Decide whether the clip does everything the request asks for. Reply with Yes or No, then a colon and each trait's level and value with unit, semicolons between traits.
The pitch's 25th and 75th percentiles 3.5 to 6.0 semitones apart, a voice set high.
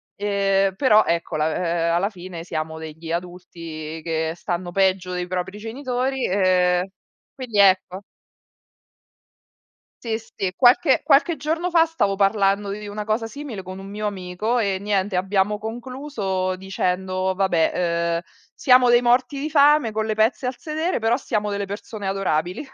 Yes: average, 4.4 semitones; high, 195 Hz